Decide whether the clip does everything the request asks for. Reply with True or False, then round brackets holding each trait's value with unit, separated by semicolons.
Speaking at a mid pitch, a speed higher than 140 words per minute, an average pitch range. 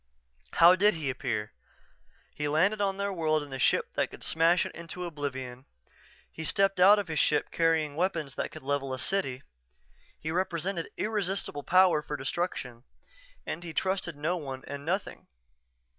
True (165 Hz; 170 wpm; 4.6 semitones)